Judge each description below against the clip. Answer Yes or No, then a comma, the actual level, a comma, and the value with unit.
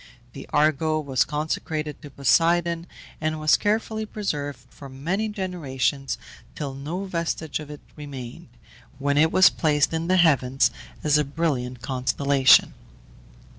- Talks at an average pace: No, slow, 130 wpm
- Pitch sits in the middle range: Yes, medium, 150 Hz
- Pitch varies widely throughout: No, average, 3.3 semitones